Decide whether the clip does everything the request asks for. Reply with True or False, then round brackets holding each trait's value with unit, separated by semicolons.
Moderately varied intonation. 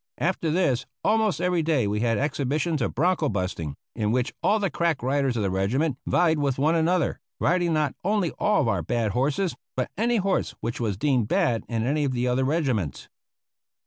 False (6.2 semitones)